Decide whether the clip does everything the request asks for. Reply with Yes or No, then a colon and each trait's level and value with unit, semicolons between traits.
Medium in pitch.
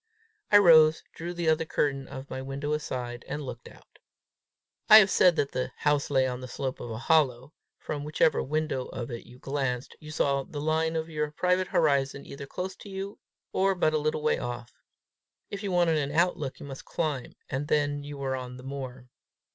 Yes: medium, 145 Hz